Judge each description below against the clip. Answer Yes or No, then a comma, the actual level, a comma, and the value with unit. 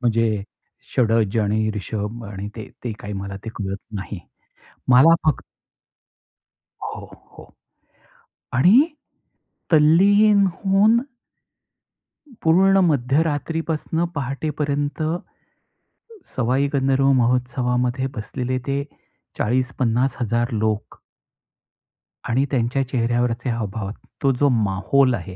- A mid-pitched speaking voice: No, low, 125 Hz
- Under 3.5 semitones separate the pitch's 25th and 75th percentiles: No, average, 4.3 semitones